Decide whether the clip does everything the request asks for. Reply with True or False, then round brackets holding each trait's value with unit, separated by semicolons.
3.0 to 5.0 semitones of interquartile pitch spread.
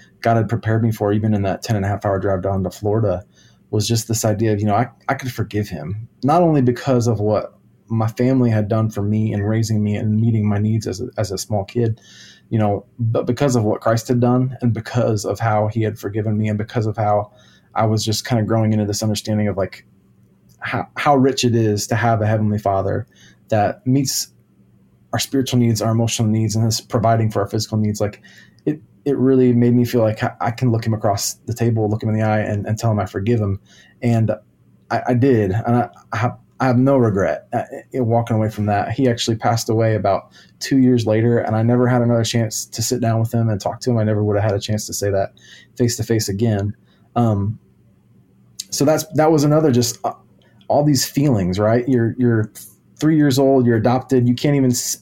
False (2.5 semitones)